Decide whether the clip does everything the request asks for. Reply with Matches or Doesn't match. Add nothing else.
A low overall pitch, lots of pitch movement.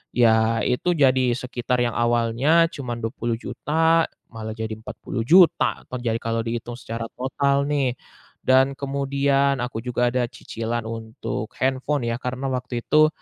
Doesn't match